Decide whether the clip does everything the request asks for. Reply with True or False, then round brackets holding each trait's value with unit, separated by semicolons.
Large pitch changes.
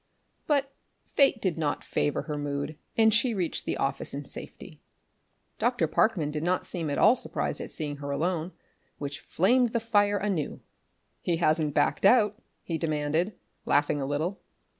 True (6.0 semitones)